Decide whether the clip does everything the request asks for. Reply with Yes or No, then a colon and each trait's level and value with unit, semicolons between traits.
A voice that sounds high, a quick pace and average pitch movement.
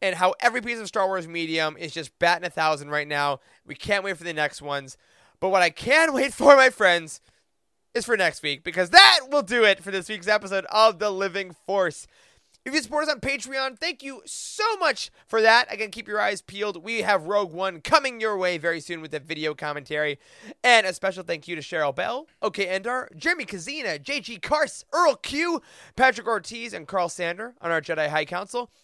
No: high, 195 Hz; fast, 215 wpm; wide, 6.4 semitones